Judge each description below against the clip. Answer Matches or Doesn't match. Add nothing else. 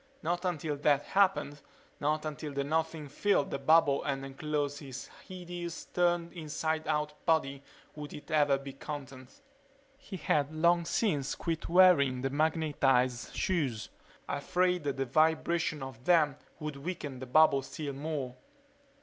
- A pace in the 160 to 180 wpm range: Doesn't match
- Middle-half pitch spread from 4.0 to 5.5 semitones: Doesn't match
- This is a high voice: Doesn't match